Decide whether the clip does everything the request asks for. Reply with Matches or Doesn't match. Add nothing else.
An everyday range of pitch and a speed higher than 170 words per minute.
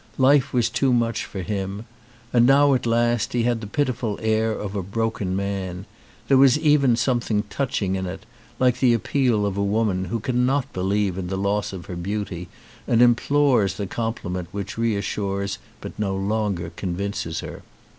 Matches